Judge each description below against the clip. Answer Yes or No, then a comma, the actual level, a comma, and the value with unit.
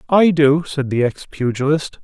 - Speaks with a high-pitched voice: No, medium, 145 Hz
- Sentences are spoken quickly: No, average, 175 wpm